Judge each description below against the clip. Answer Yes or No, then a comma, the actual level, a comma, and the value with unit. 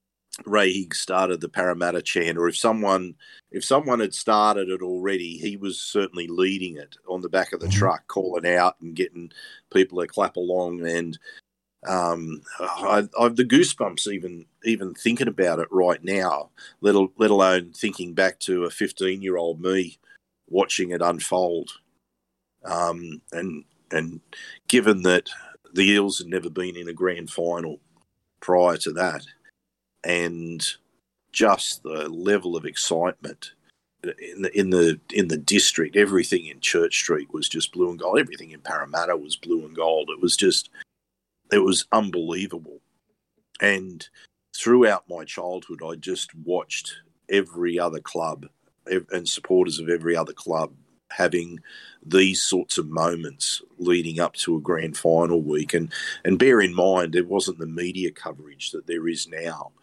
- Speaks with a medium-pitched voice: No, very low, 90 Hz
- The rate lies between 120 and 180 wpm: Yes, average, 155 wpm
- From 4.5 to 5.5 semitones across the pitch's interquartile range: No, narrow, 2.6 semitones